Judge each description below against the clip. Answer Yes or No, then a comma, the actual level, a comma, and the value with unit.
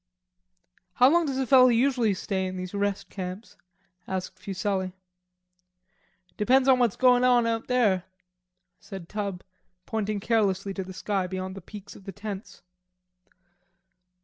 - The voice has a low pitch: No, high, 205 Hz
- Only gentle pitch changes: No, average, 4.2 semitones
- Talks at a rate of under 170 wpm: Yes, average, 140 wpm